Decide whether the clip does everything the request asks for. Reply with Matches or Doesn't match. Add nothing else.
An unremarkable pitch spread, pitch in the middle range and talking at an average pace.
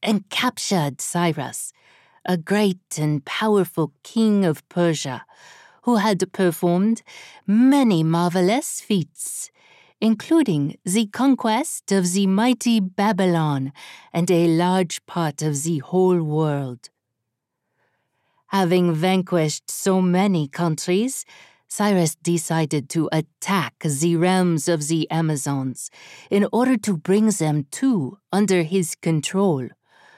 Doesn't match